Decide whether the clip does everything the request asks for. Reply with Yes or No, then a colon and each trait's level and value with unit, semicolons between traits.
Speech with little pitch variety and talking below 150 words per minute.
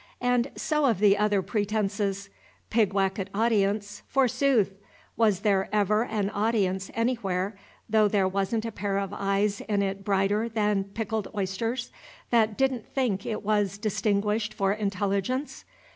Yes: narrow, 2.1 semitones; average, 140 wpm